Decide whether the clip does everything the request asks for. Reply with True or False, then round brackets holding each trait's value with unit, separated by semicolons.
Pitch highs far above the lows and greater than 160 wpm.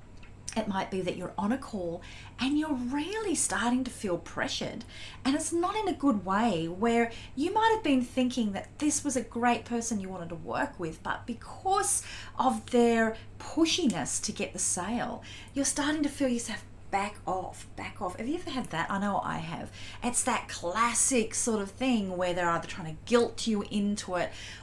True (6.4 semitones; 195 wpm)